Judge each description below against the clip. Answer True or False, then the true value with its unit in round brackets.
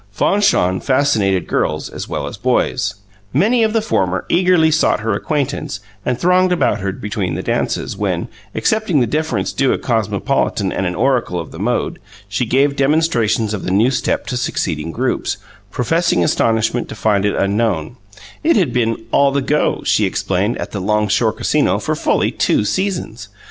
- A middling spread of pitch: False (6.9 semitones)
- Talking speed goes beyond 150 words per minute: True (175 wpm)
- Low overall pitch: True (115 Hz)